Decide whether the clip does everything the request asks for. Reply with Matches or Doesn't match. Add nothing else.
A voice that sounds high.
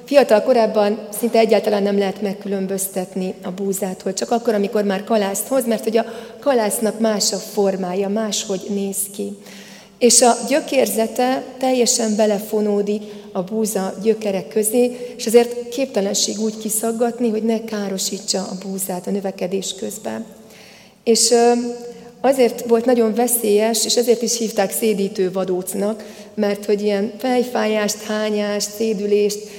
Matches